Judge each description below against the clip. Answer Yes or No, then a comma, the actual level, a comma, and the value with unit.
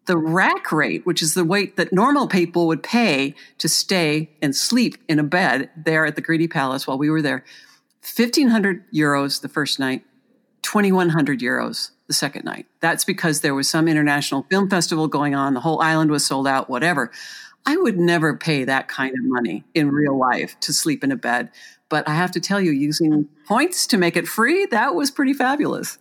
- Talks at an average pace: No, fast, 210 wpm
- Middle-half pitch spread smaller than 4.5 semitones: No, average, 5.3 semitones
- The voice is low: No, medium, 160 Hz